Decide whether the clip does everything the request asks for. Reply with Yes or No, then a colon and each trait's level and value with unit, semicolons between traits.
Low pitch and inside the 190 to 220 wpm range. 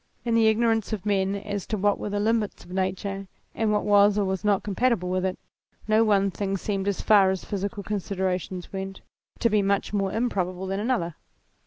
No: high, 200 Hz; fast, 205 wpm